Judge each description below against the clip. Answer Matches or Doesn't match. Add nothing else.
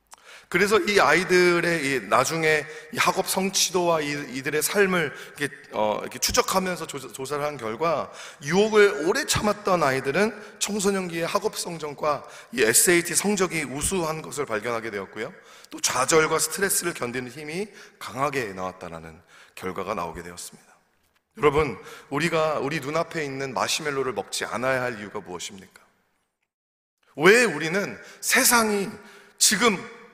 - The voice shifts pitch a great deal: Matches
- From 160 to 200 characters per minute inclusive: Doesn't match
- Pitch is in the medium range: Matches